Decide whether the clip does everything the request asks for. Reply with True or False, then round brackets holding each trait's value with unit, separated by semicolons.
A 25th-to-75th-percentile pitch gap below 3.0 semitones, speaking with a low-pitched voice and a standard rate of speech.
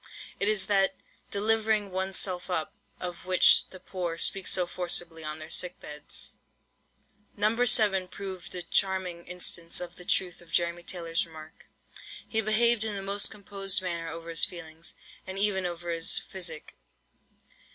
False (2.6 semitones; 180 Hz; 155 wpm)